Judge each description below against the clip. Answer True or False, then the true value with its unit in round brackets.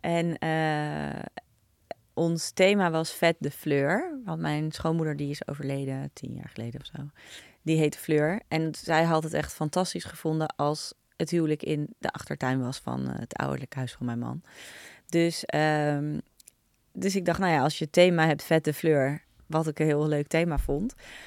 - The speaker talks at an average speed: True (185 wpm)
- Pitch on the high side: False (155 Hz)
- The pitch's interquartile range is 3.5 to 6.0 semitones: False (2.7 semitones)